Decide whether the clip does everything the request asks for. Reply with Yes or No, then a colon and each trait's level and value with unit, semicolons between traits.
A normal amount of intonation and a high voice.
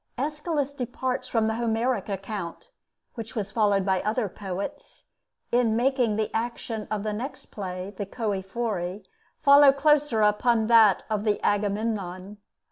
Yes: average, 3.3 semitones; high, 220 Hz